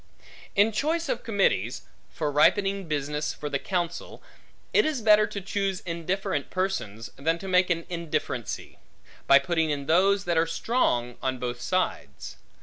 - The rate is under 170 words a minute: Yes, average, 150 wpm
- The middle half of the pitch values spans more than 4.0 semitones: Yes, wide, 5.4 semitones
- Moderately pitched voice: Yes, medium, 170 Hz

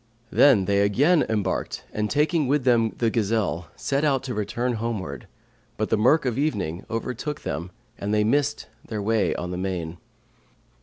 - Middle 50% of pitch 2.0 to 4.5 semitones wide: No, average, 5.1 semitones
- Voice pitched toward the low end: Yes, low, 110 Hz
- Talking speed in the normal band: Yes, average, 165 wpm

